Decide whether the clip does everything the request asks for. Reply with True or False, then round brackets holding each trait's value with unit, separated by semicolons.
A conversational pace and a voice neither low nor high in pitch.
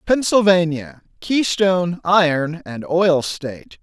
False (95 wpm; 175 Hz)